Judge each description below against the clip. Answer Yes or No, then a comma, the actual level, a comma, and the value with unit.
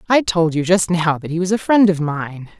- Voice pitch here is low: No, medium, 175 Hz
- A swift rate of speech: Yes, fast, 275 wpm